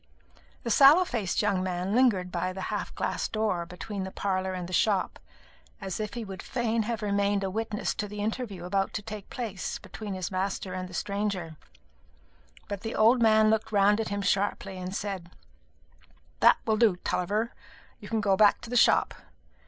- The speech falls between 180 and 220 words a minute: Yes, average, 185 wpm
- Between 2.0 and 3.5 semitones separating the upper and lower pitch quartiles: Yes, average, 2.7 semitones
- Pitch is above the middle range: Yes, high, 205 Hz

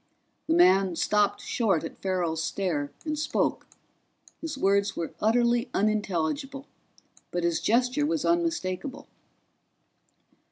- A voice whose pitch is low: No, high, 210 Hz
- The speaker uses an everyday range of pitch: No, wide, 7.1 semitones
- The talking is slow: Yes, slow, 110 wpm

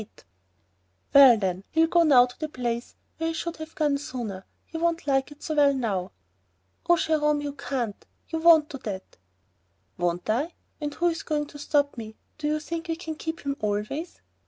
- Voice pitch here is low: No, very high, 290 Hz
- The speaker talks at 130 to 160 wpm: No, average, 195 wpm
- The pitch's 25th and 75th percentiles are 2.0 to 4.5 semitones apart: No, average, 5.1 semitones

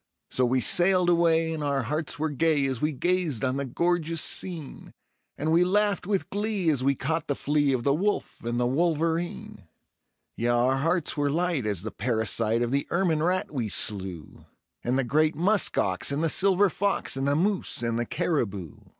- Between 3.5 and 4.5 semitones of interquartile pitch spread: No, wide, 5.5 semitones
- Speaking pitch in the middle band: Yes, medium, 150 Hz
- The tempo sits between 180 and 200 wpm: Yes, average, 195 wpm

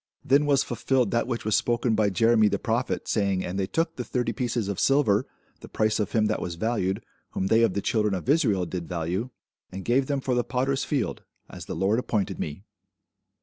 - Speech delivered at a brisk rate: Yes, fast, 215 wpm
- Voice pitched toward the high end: No, low, 110 Hz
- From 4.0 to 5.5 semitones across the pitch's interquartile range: Yes, average, 4.3 semitones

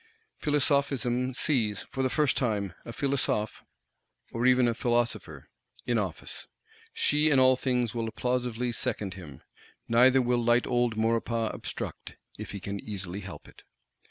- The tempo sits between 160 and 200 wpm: No, average, 145 wpm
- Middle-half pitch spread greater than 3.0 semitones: No, average, 2.7 semitones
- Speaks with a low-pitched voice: Yes, low, 120 Hz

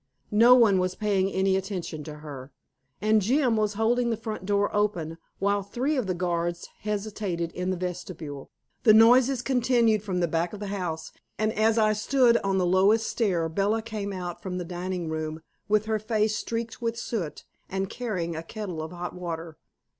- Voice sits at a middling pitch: No, high, 200 Hz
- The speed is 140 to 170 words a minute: No, average, 185 wpm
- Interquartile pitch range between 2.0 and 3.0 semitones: No, average, 3.8 semitones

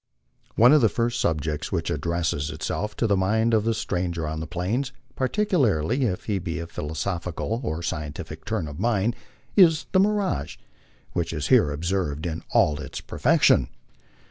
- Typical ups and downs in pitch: No, wide, 6.7 semitones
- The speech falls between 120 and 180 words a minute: Yes, average, 170 wpm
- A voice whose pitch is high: No, very low, 90 Hz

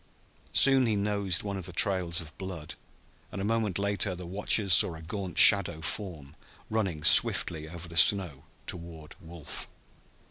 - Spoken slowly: No, average, 155 wpm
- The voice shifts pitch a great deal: No, average, 3.4 semitones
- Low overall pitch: Yes, very low, 90 Hz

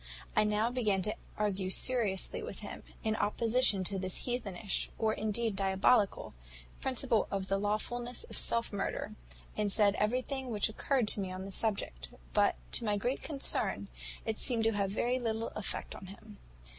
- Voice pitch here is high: Yes, high, 215 Hz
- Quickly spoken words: No, average, 170 wpm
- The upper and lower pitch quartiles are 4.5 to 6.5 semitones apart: No, average, 3.2 semitones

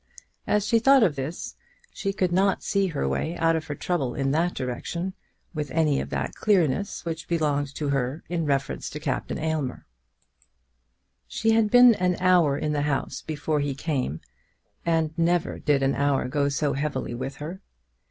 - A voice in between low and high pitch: Yes, medium, 155 Hz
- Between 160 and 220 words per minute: Yes, average, 175 wpm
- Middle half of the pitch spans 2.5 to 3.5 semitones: No, average, 4.1 semitones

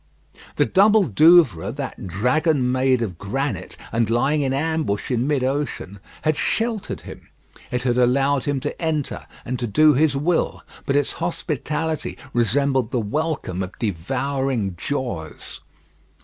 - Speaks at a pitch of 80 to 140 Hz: Yes, low, 135 Hz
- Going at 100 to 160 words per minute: Yes, average, 140 wpm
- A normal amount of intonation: Yes, average, 4.4 semitones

